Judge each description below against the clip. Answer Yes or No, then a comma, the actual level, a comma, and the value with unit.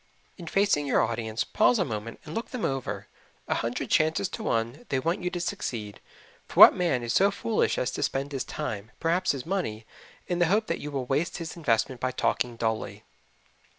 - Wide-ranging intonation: Yes, wide, 7.2 semitones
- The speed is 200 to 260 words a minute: Yes, fast, 205 wpm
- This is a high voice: No, medium, 145 Hz